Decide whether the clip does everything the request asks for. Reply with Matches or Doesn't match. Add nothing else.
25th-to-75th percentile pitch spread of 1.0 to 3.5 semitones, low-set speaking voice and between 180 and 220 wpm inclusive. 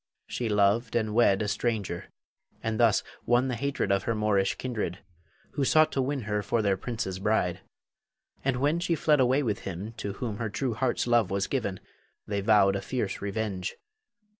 Doesn't match